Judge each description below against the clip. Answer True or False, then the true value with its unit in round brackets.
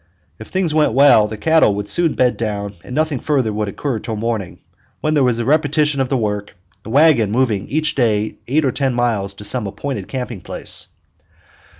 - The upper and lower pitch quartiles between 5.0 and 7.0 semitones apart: True (5.3 semitones)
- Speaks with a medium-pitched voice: False (125 Hz)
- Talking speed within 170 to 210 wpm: True (200 wpm)